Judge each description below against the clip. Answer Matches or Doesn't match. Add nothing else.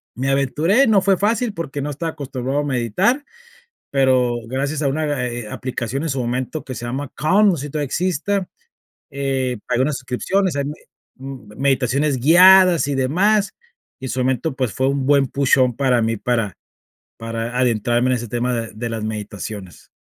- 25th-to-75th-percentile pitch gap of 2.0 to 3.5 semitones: Doesn't match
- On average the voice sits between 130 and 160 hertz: Matches